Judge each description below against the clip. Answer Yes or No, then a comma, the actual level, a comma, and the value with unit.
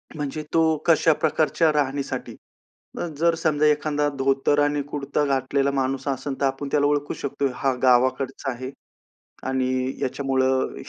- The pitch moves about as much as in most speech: No, narrow, 1.8 semitones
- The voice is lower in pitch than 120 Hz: No, medium, 140 Hz